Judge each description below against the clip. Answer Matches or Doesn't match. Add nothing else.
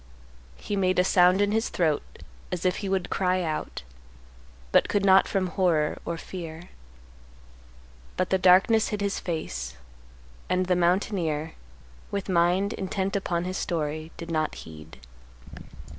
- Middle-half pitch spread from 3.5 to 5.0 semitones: Doesn't match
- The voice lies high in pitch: Doesn't match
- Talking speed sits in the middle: Matches